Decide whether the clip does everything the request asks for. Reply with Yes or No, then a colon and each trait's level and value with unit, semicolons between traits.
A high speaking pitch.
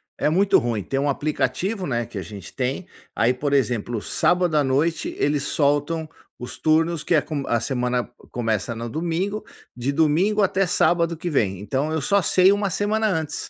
No: medium, 150 Hz